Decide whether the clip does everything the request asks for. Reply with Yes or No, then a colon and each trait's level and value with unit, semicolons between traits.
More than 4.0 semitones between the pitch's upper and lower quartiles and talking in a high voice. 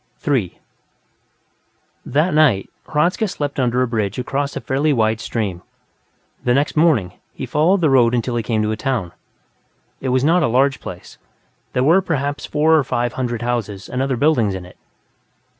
No: average, 4.4 semitones; low, 130 Hz